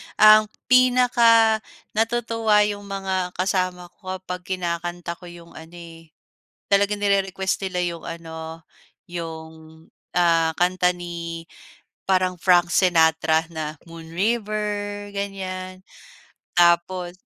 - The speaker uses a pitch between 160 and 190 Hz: Yes, medium, 185 Hz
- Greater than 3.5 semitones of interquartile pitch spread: No, average, 3.1 semitones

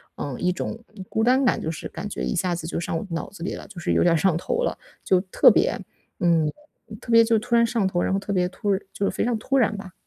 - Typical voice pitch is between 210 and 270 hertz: No, high, 190 Hz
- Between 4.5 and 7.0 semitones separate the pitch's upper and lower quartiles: Yes, average, 5.0 semitones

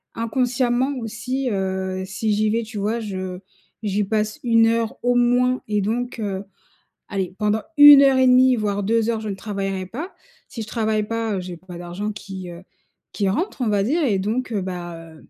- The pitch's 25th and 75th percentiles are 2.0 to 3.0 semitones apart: No, average, 3.8 semitones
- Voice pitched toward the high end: Yes, high, 215 Hz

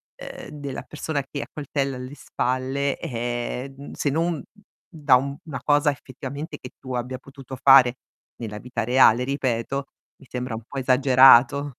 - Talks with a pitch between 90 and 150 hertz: Yes, low, 135 Hz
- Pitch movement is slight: Yes, narrow, 2.0 semitones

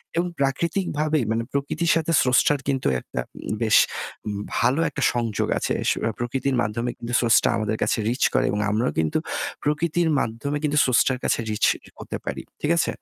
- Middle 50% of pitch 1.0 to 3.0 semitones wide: No, average, 4.5 semitones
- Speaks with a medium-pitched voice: No, low, 130 Hz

